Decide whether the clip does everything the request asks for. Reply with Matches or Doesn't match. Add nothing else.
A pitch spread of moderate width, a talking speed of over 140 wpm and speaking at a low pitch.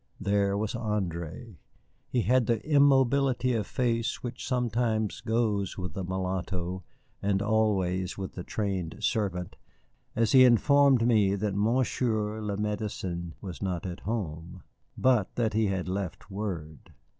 Doesn't match